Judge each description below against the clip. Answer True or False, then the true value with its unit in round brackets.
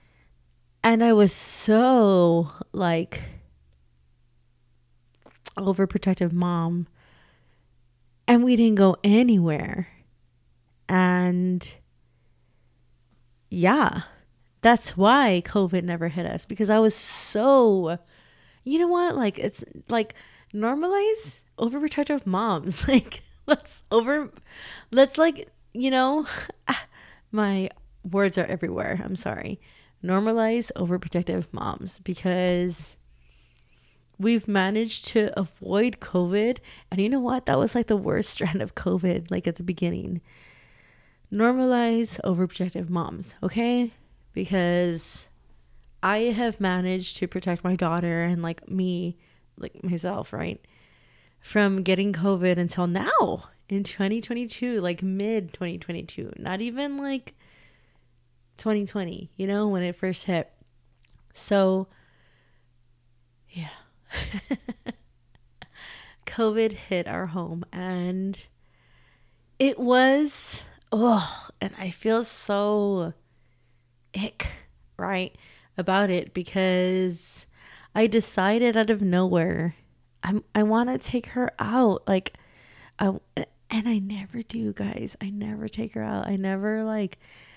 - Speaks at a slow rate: True (105 wpm)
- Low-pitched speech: False (190 Hz)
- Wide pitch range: False (4.7 semitones)